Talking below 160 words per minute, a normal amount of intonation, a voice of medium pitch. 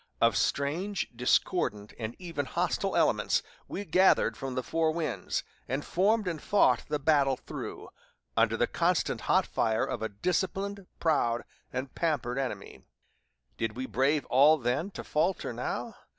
No: average, 150 wpm; wide, 5.7 semitones; medium, 145 Hz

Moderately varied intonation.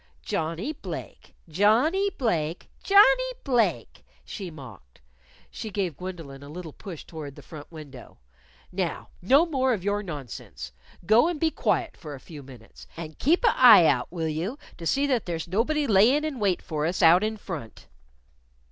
No: wide, 8.7 semitones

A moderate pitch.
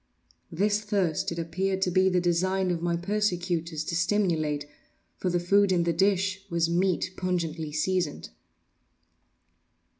Yes: medium, 180 Hz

